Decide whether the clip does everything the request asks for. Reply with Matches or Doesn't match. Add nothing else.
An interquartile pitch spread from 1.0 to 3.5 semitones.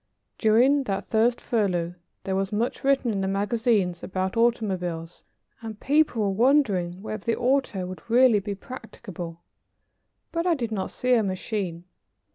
Doesn't match